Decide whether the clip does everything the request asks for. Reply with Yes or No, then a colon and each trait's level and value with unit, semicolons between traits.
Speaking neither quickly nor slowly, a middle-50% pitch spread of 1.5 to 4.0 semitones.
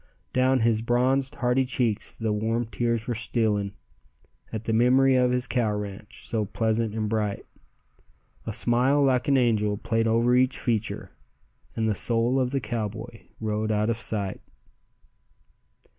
Yes: average, 150 wpm; narrow, 2.4 semitones